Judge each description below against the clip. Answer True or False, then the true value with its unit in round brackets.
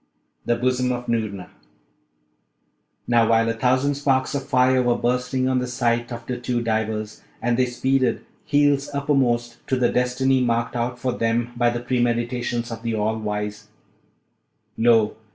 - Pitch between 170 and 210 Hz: False (120 Hz)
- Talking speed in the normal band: True (155 wpm)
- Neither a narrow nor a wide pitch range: False (1.6 semitones)